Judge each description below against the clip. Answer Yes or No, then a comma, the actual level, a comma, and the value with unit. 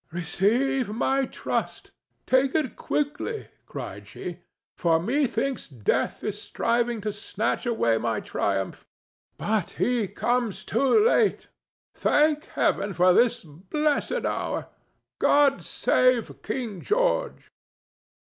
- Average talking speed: No, slow, 110 wpm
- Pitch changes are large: Yes, wide, 6.3 semitones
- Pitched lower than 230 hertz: No, high, 235 Hz